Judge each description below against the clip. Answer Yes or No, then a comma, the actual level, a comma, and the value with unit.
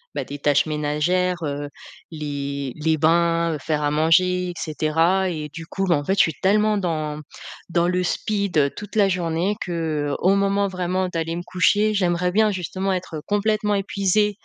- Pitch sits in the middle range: Yes, medium, 175 Hz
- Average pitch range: Yes, average, 3.8 semitones